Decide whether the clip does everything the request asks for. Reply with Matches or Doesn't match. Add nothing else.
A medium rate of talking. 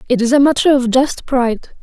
Doesn't match